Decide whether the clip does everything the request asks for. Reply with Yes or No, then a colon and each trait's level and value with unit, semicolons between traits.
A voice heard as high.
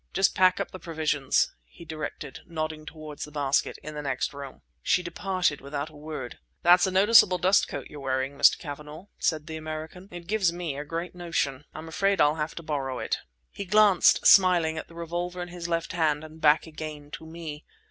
No: medium, 160 Hz